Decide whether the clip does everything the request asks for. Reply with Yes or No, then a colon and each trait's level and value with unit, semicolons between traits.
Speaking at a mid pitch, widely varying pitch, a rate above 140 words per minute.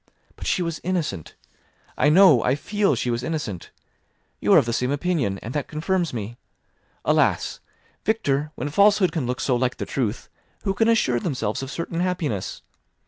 Yes: medium, 145 Hz; wide, 6.6 semitones; average, 175 wpm